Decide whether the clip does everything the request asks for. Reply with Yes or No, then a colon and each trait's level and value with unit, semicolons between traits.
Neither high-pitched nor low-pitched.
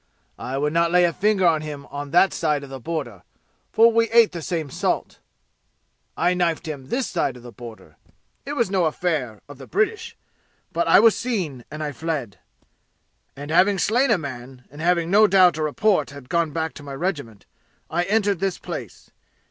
Yes: medium, 165 Hz